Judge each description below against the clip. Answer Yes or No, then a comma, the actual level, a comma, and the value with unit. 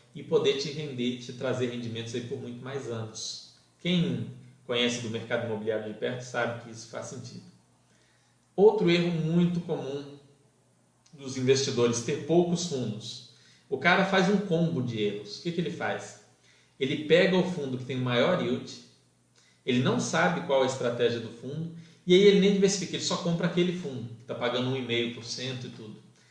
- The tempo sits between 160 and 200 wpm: Yes, average, 180 wpm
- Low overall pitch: Yes, low, 130 Hz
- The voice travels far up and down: Yes, wide, 6.2 semitones